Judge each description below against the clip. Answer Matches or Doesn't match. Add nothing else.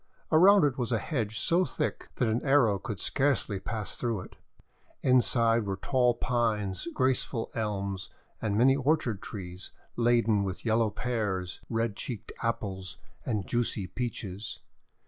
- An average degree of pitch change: Matches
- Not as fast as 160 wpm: Matches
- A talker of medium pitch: Doesn't match